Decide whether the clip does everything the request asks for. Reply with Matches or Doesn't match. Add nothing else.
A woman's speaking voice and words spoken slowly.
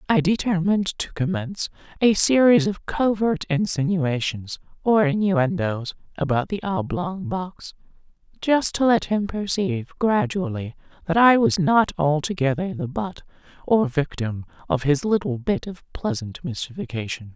Matches